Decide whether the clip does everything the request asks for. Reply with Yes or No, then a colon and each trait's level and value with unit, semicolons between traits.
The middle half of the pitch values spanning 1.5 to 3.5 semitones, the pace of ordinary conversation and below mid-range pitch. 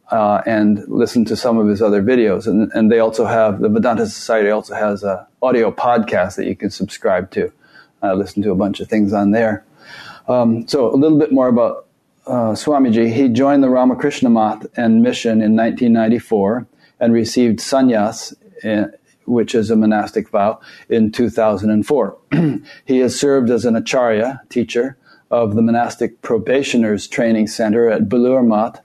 Yes: average, 2.8 semitones; average, 170 wpm; low, 115 Hz